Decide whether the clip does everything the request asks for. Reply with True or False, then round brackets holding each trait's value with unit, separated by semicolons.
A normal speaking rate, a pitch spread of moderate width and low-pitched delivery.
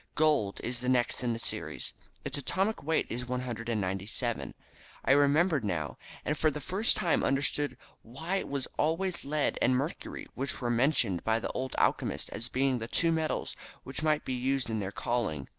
True (180 wpm; 4.6 semitones; 130 Hz)